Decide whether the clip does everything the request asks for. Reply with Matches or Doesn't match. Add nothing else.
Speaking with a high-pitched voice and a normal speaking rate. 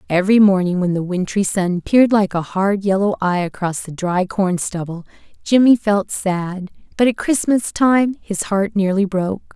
Matches